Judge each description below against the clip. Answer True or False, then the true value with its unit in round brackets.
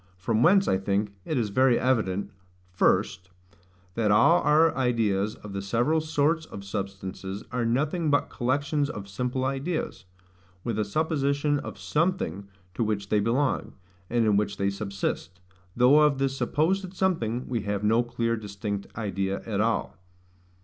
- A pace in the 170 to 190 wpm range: False (155 wpm)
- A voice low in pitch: True (115 Hz)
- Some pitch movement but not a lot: False (6.0 semitones)